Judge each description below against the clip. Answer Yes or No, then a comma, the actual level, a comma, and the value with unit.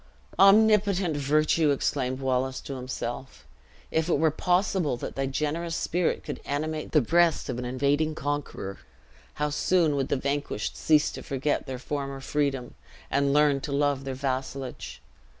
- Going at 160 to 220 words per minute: No, average, 150 wpm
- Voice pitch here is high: No, medium, 145 Hz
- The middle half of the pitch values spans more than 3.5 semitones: No, average, 2.8 semitones